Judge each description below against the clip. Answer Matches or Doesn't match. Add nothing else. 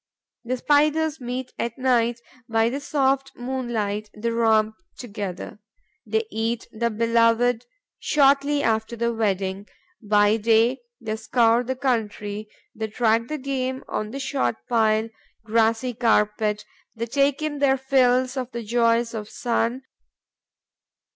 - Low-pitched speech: Doesn't match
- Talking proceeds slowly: Matches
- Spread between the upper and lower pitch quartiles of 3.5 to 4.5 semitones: Doesn't match